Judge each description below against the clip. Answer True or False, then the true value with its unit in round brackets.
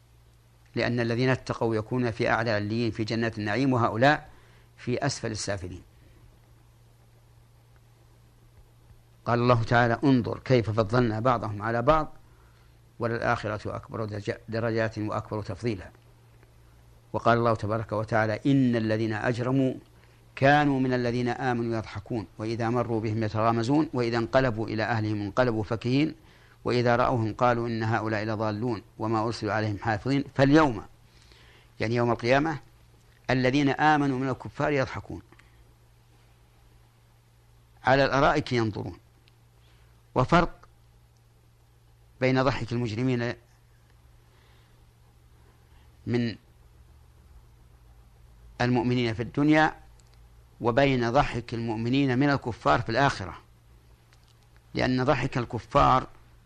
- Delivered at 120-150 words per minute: False (95 wpm)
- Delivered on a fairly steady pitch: True (2.1 semitones)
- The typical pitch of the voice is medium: False (115 Hz)